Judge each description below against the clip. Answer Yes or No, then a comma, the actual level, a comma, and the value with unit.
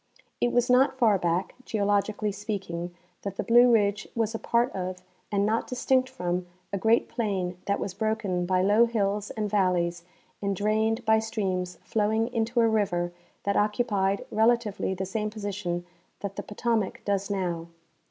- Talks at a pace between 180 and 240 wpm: No, average, 160 wpm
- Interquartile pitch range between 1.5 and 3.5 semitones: Yes, average, 2.9 semitones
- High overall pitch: Yes, high, 205 Hz